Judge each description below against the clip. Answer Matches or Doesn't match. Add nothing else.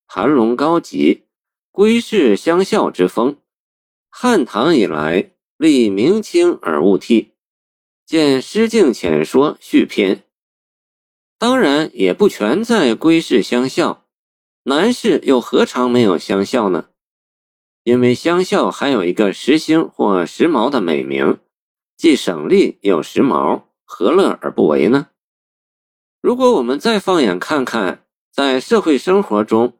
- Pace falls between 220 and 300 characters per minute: Doesn't match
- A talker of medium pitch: Matches